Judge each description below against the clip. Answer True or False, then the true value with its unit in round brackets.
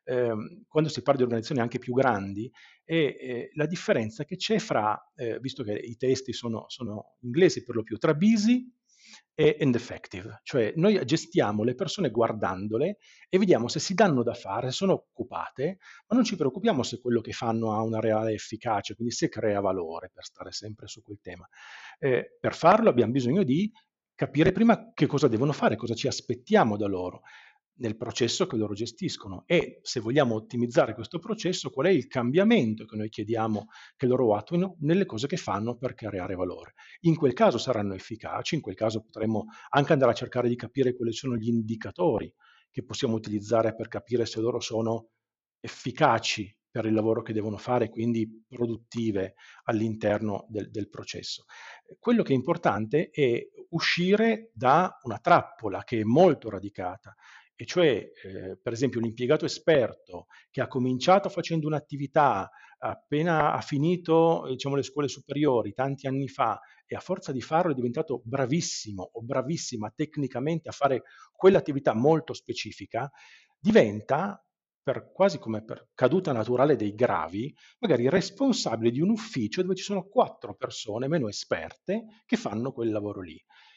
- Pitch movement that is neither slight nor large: False (6.6 semitones)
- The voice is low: True (125 Hz)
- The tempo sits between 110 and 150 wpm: False (165 wpm)